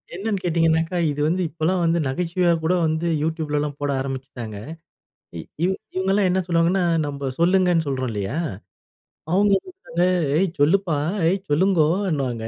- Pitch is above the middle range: No, medium, 165 Hz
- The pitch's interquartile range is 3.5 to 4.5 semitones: Yes, average, 4.0 semitones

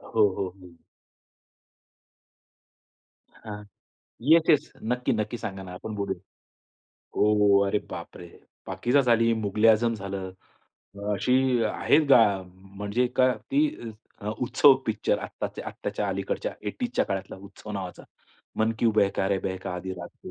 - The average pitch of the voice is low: Yes, low, 105 Hz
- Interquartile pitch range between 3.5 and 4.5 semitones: Yes, average, 3.8 semitones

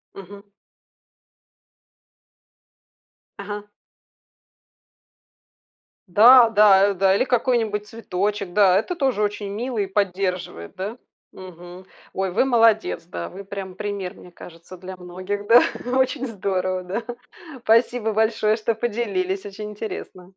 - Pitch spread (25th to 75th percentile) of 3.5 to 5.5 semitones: No, average, 3.0 semitones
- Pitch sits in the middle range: No, high, 205 Hz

